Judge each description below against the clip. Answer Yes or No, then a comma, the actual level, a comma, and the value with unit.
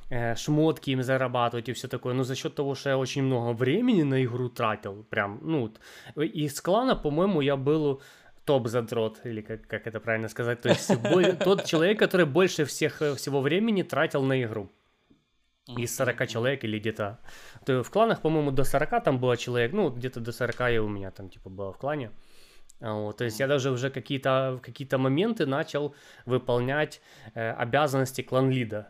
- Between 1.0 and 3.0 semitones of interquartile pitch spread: No, average, 3.8 semitones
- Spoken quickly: Yes, fast, 185 wpm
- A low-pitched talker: Yes, low, 130 Hz